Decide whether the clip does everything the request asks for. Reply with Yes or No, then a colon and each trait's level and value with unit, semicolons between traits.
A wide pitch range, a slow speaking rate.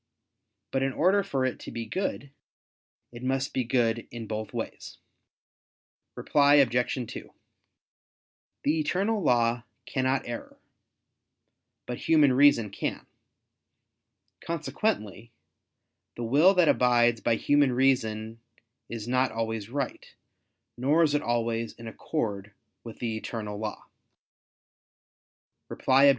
No: average, 3.7 semitones; slow, 115 wpm